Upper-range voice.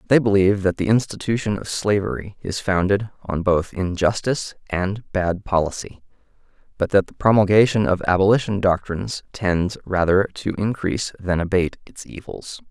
No: very low, 95 Hz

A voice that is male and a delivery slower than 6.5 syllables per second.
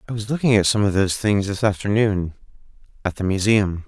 Yes: male; 6.0 syllables/s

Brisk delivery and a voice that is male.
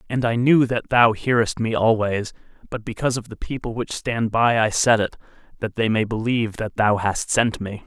Yes: fast, 215 wpm; male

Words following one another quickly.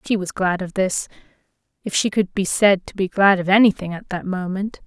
Yes: fast, 220 wpm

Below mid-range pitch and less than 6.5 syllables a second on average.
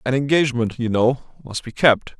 Yes: low, 125 Hz; 5.5 syllables/s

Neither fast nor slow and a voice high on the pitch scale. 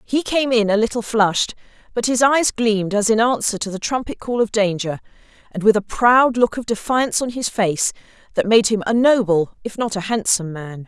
No: fast, 215 wpm; high, 220 Hz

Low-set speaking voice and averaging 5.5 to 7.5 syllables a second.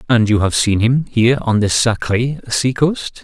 No: low, 120 Hz; 4.8 syllables/s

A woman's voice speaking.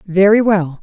Yes: female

